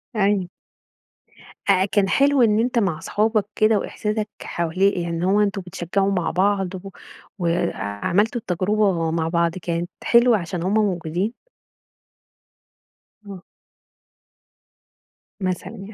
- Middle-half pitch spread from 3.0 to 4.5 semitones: Yes, average, 3.3 semitones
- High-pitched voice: Yes, high, 195 Hz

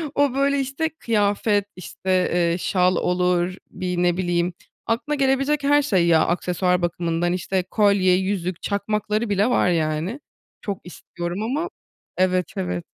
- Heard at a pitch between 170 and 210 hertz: Yes, medium, 185 Hz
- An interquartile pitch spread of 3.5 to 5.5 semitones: Yes, average, 4.4 semitones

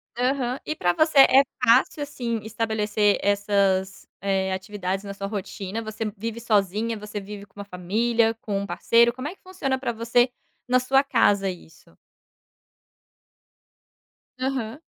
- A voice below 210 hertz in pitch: No, high, 220 Hz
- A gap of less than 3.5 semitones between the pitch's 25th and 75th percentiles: No, average, 3.8 semitones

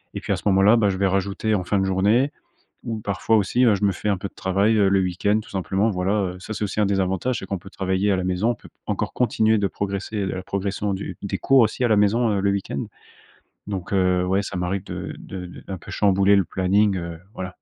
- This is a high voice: No, low, 100 Hz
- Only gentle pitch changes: Yes, narrow, 1.8 semitones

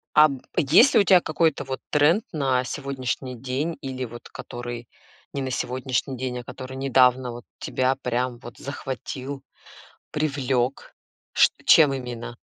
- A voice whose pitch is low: Yes, low, 130 Hz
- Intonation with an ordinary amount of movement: No, narrow, 2.1 semitones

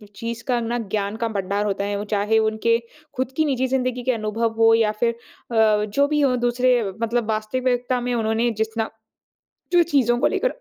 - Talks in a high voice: Yes, high, 230 Hz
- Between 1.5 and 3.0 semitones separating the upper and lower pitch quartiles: Yes, narrow, 2.6 semitones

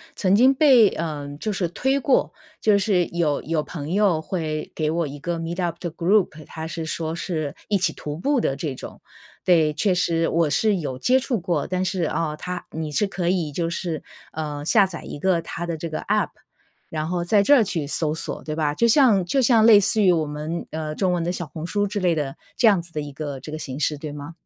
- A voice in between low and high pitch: Yes, medium, 170 Hz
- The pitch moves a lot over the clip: No, average, 4.0 semitones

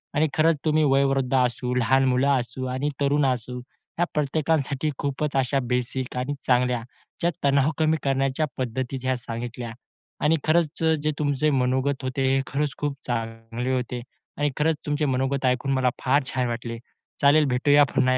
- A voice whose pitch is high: No, low, 135 Hz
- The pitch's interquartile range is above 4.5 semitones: No, average, 2.7 semitones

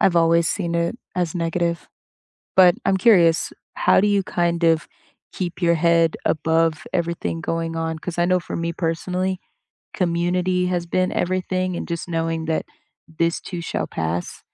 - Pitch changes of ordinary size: No, narrow, 1.6 semitones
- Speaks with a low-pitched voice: No, medium, 170 Hz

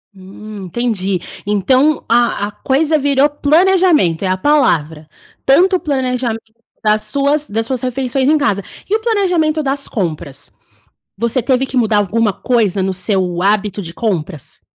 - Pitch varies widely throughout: Yes, wide, 6.4 semitones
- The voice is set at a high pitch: Yes, high, 235 Hz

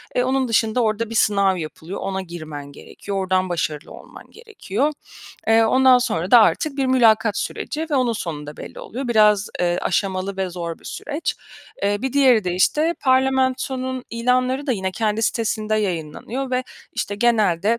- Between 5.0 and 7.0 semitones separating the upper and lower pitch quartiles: Yes, wide, 5.4 semitones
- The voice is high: Yes, high, 220 Hz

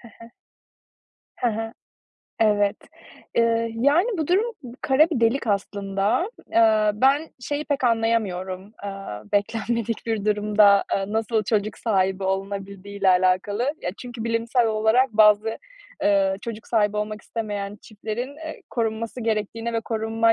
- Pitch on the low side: No, high, 220 Hz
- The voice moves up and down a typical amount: No, narrow, 2.3 semitones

